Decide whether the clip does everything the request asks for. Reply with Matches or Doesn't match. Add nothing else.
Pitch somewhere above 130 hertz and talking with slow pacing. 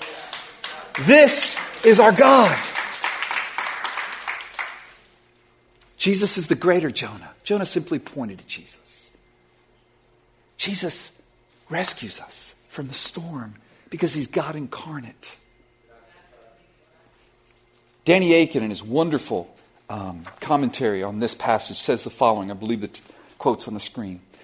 Matches